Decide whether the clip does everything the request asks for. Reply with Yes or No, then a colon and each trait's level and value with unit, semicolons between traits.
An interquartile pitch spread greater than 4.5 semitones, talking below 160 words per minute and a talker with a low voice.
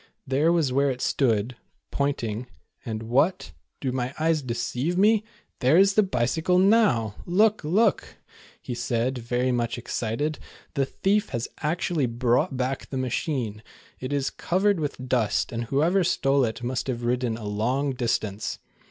Yes: average, 5.2 semitones; average, 150 wpm; low, 130 Hz